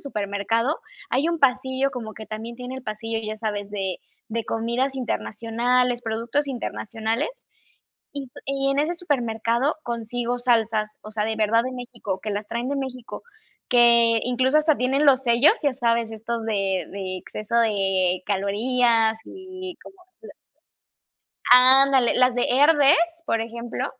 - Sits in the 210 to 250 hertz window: Yes, high, 235 Hz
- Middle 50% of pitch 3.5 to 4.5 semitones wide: No, average, 3.0 semitones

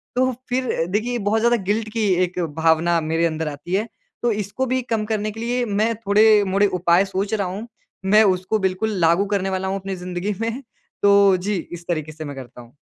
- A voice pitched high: Yes, high, 200 Hz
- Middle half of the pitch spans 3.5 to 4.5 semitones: Yes, average, 3.8 semitones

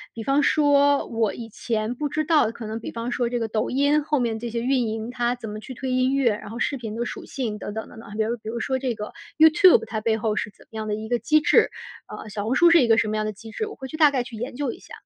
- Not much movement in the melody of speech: No, average, 3.8 semitones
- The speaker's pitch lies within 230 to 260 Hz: Yes, high, 235 Hz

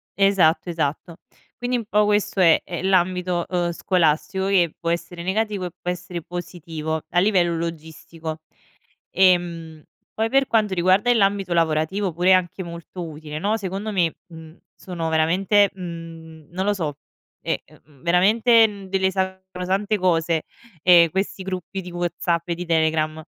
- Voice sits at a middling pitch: Yes, medium, 180 Hz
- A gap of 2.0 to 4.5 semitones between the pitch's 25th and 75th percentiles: Yes, average, 2.7 semitones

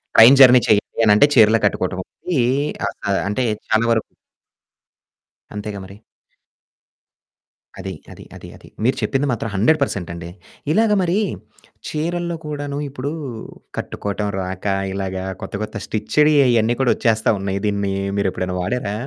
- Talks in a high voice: No, low, 110 Hz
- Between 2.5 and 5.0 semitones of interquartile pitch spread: No, wide, 5.6 semitones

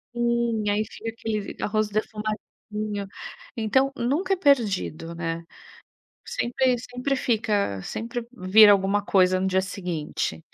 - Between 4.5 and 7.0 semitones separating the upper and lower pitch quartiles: No, average, 3.8 semitones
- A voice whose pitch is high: Yes, high, 215 Hz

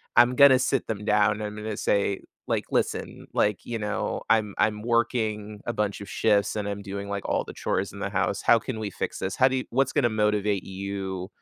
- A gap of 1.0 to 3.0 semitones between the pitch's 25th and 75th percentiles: Yes, narrow, 2.5 semitones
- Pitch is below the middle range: Yes, low, 105 Hz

